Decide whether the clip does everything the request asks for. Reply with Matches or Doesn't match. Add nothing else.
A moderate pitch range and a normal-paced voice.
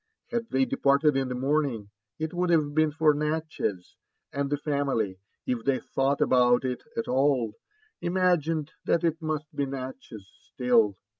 Matches